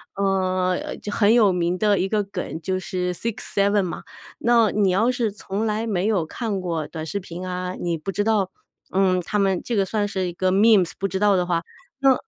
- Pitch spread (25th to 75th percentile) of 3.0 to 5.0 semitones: No, narrow, 2.5 semitones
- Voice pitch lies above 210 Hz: No, high, 195 Hz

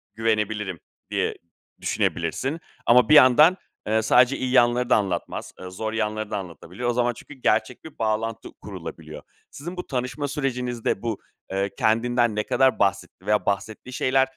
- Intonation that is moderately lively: Yes, average, 3.1 semitones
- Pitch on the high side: No, low, 120 Hz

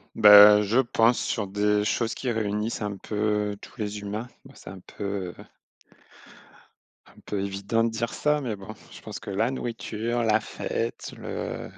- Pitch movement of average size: No, narrow, 2.0 semitones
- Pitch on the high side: No, low, 105 Hz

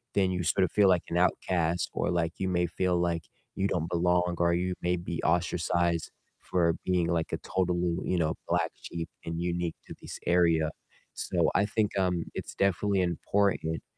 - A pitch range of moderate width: No, narrow, 1.5 semitones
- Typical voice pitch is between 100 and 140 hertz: No, very low, 85 Hz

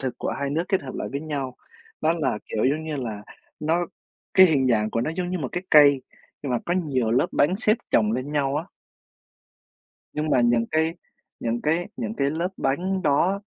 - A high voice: No, medium, 145 Hz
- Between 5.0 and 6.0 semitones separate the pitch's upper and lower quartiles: No, average, 4.6 semitones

